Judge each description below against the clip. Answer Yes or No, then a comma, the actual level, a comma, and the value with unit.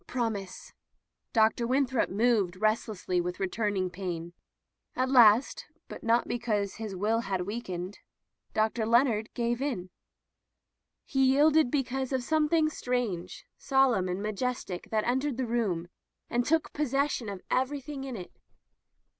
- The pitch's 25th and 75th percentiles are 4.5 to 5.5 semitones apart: Yes, average, 4.8 semitones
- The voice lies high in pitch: Yes, high, 235 Hz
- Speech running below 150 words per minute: Yes, average, 140 wpm